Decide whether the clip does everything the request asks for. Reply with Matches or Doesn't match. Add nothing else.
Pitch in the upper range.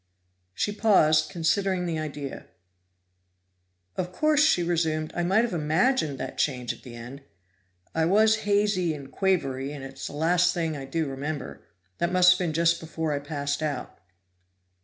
Doesn't match